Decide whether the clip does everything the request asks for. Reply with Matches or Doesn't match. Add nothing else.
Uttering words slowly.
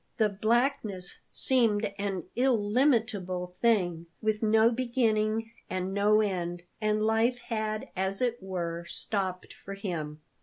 Matches